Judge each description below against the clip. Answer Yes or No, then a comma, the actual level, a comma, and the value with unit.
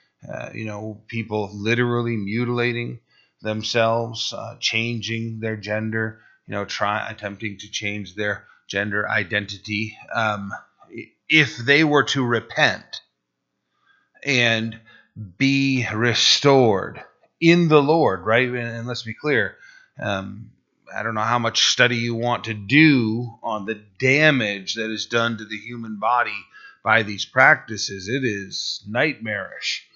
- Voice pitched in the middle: No, low, 115 Hz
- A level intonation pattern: Yes, narrow, 2.2 semitones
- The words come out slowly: Yes, slow, 130 wpm